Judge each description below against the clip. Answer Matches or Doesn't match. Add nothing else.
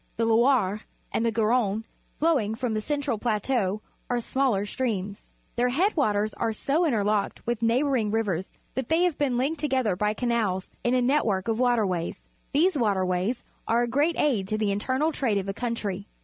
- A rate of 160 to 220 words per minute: Matches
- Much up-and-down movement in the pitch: Doesn't match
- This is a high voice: Matches